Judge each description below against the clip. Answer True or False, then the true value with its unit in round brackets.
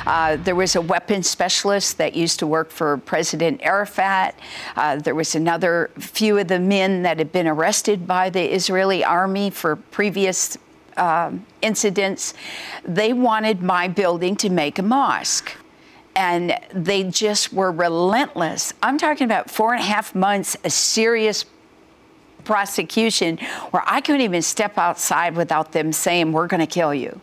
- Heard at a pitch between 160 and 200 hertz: True (190 Hz)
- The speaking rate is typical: True (155 wpm)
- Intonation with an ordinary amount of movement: True (3.3 semitones)